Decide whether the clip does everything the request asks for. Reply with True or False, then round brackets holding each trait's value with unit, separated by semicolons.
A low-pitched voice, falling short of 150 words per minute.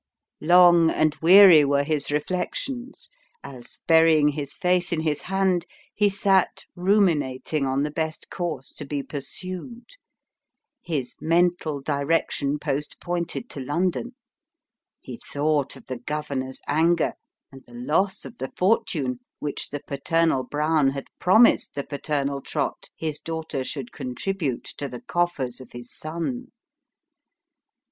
False (155 Hz; 135 wpm)